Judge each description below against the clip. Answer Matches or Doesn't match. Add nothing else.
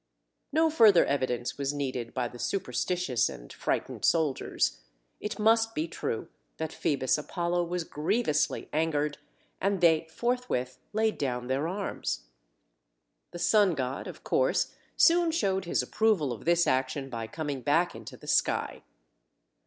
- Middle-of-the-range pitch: Matches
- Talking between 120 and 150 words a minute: Matches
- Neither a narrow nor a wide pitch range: Doesn't match